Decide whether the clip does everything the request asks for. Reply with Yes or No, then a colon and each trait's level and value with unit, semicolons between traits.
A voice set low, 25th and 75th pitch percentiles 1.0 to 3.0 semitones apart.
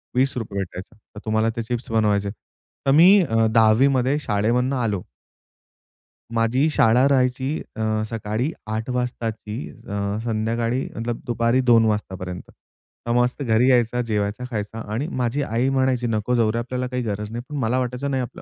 Yes: low, 115 Hz; narrow, 2.6 semitones